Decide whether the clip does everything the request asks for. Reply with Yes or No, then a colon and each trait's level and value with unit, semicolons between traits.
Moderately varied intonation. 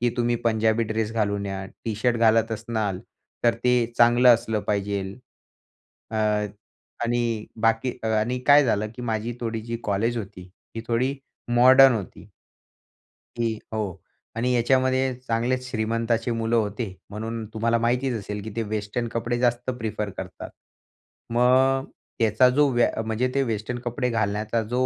No: narrow, 2.1 semitones